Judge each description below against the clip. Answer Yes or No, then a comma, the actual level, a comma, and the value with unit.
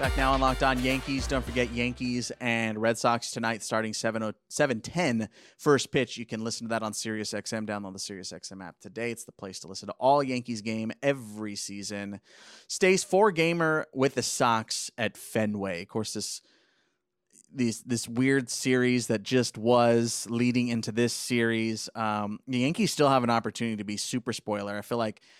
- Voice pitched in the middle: No, low, 115 Hz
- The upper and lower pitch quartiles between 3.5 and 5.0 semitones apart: No, average, 2.7 semitones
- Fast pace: No, average, 185 wpm